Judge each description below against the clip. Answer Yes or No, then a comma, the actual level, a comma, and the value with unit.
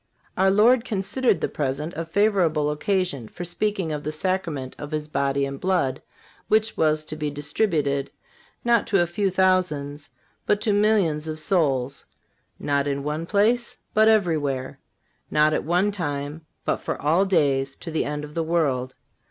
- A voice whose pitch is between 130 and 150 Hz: No, medium, 160 Hz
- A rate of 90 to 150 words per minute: No, average, 165 wpm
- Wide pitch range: No, average, 5.0 semitones